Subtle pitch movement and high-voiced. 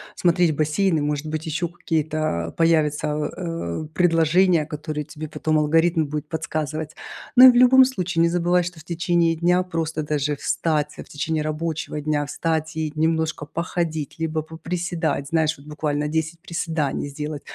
No: narrow, 1.9 semitones; medium, 160 Hz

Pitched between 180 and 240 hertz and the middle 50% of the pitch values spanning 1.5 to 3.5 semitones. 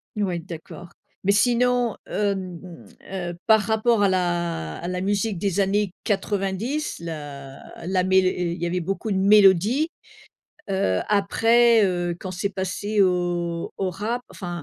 Yes: high, 190 Hz; average, 3.1 semitones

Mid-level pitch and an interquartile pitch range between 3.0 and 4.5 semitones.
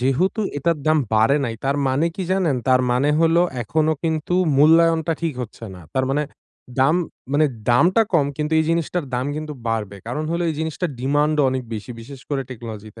Yes: medium, 150 Hz; average, 4.1 semitones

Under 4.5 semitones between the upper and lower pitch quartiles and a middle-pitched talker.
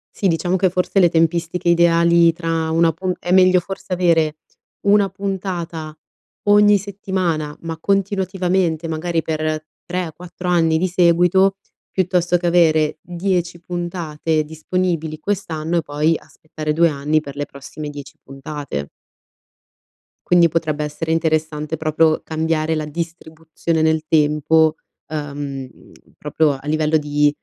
Yes: narrow, 2.4 semitones; medium, 165 Hz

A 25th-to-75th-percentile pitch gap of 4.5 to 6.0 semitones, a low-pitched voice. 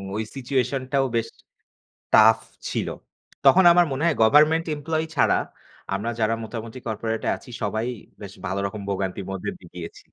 Yes: average, 5.1 semitones; low, 115 Hz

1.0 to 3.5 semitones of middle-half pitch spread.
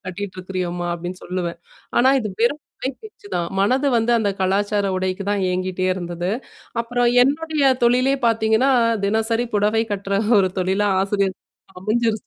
No: average, 4.3 semitones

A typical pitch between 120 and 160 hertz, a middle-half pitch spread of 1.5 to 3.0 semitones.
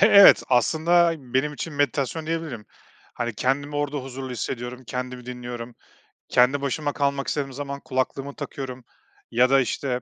Yes: low, 135 Hz; narrow, 2.6 semitones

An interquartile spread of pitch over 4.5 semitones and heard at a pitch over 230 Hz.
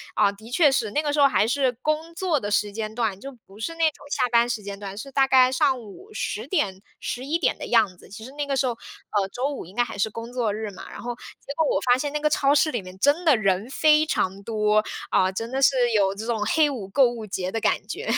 Yes: average, 5.2 semitones; high, 240 Hz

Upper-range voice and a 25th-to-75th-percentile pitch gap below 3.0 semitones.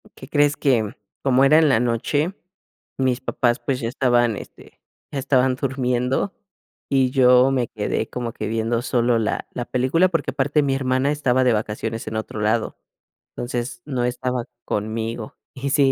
No: low, 125 Hz; narrow, 2.5 semitones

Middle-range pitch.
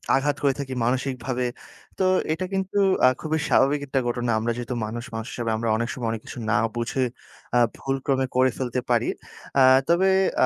No: low, 130 Hz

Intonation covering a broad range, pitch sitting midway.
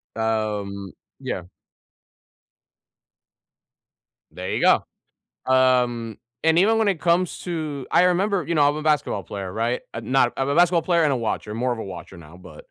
No: wide, 7.6 semitones; low, 130 Hz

